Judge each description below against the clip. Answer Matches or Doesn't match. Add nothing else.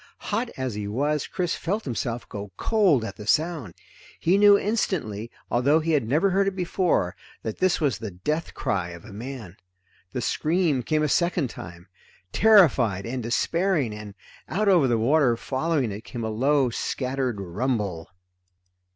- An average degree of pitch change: Doesn't match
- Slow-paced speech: Doesn't match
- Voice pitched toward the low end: Matches